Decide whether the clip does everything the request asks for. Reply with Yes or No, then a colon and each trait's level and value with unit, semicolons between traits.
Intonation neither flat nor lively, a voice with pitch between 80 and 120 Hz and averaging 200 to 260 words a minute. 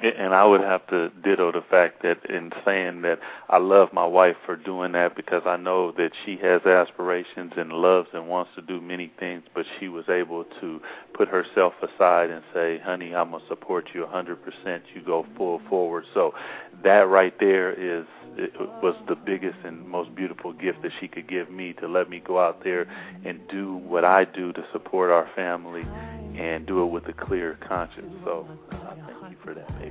No: narrow, 1.4 semitones; very low, 90 Hz; fast, 205 wpm